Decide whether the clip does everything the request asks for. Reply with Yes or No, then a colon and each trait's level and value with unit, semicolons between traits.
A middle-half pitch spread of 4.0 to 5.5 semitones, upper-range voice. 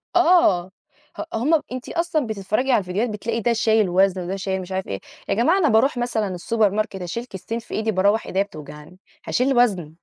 Yes: average, 4.4 semitones; high, 215 Hz